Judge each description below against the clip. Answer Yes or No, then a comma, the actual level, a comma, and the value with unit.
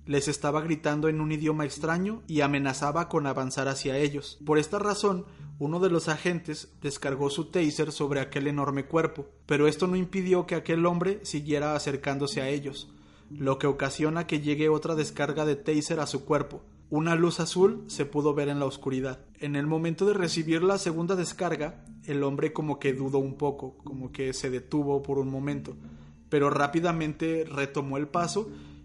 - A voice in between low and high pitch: Yes, medium, 150 Hz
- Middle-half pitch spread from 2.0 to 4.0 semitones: Yes, average, 2.8 semitones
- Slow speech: No, average, 180 wpm